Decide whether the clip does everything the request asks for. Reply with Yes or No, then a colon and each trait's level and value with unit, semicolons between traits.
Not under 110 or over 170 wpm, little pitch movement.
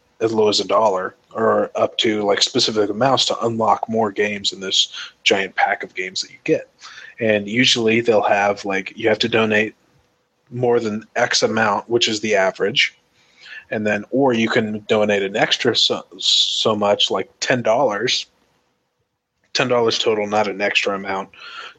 Yes: average, 165 wpm; narrow, 1.7 semitones